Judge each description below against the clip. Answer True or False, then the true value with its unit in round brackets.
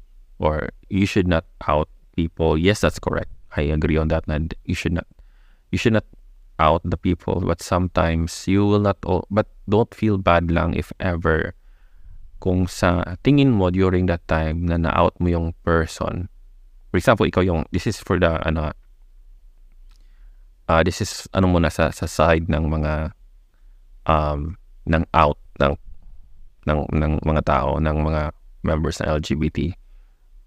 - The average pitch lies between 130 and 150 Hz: False (85 Hz)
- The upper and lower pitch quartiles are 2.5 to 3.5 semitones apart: True (2.8 semitones)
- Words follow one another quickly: True (160 wpm)